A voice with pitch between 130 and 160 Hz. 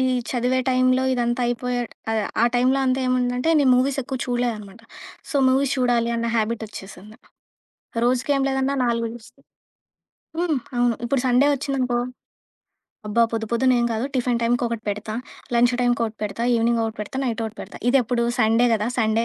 No: high, 240 Hz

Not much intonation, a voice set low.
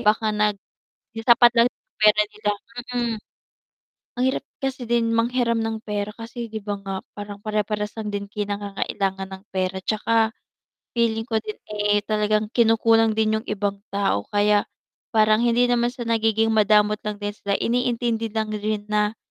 No: narrow, 1.7 semitones; high, 215 Hz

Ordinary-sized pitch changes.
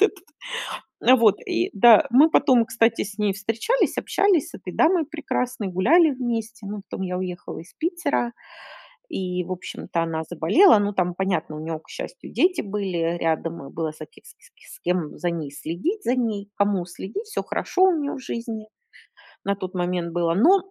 No: wide, 6.6 semitones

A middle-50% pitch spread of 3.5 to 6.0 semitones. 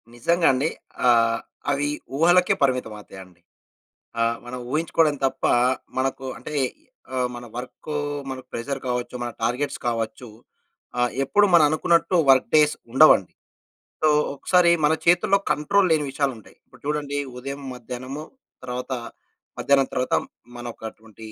Yes: average, 3.8 semitones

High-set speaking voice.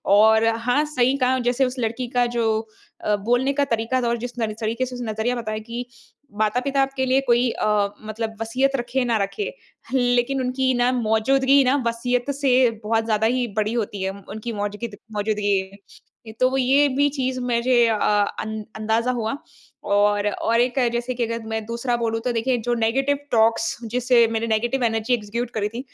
Yes: high, 235 Hz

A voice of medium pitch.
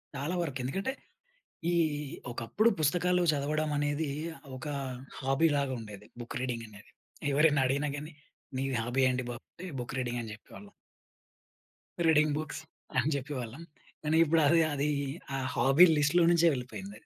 Yes: medium, 145 Hz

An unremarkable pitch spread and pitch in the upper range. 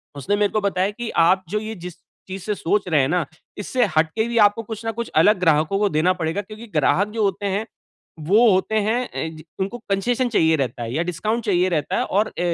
Yes: average, 4.5 semitones; high, 195 Hz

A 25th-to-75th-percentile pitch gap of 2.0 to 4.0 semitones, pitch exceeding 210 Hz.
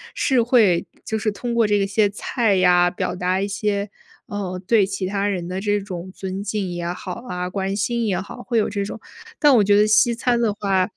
No: narrow, 2.5 semitones; high, 200 Hz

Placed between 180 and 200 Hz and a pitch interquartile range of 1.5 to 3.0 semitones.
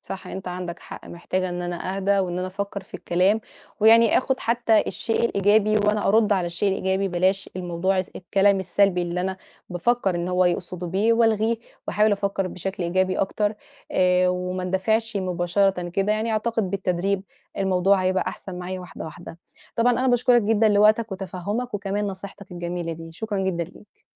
Yes: high, 190 Hz; narrow, 2.6 semitones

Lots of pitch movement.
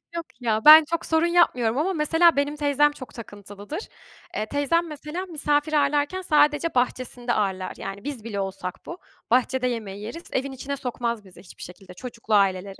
Yes: wide, 6.1 semitones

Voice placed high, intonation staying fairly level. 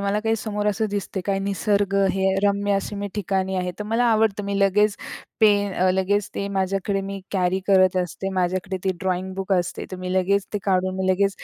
Yes: high, 195 Hz; narrow, 1.4 semitones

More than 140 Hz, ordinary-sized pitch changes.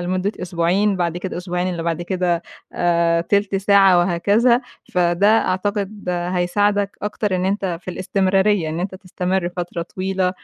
No: medium, 185 Hz; narrow, 2.3 semitones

